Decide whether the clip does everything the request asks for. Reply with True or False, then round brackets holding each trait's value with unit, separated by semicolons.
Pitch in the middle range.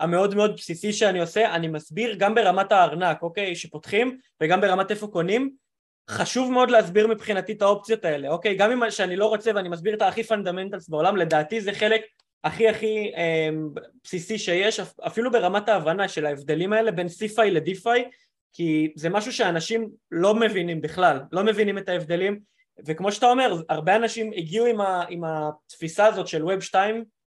False (200 Hz)